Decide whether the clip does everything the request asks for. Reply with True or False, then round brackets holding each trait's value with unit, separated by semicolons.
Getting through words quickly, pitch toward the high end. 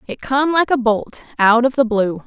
True (240 wpm; 240 Hz)